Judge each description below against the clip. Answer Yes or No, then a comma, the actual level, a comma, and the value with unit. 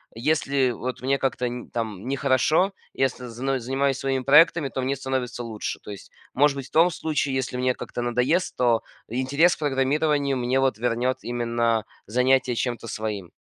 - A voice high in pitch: No, low, 130 Hz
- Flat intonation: Yes, narrow, 2.3 semitones